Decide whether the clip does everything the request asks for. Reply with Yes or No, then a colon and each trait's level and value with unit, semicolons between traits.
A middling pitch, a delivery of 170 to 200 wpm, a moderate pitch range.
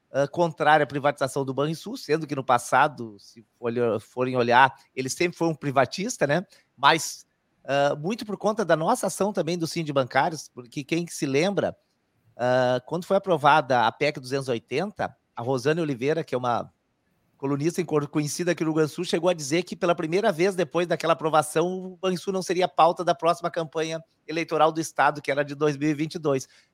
Yes: medium, 155 Hz; average, 180 wpm; average, 3.8 semitones